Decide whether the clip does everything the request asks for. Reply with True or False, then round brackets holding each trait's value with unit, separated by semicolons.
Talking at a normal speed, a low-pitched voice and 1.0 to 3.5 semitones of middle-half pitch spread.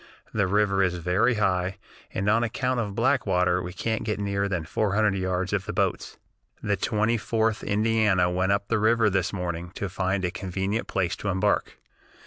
True (185 wpm; 100 Hz; 2.8 semitones)